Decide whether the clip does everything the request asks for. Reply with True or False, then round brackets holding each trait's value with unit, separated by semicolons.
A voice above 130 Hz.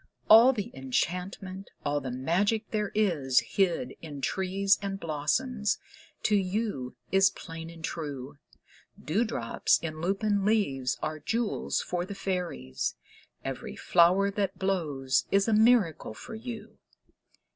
True (185 Hz)